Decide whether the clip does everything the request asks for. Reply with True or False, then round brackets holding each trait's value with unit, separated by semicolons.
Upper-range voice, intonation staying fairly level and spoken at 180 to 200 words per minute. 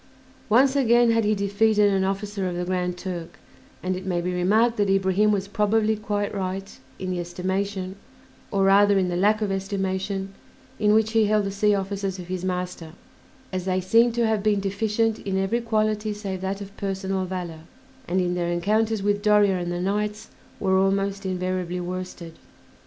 True (195 Hz; 2.2 semitones; 185 wpm)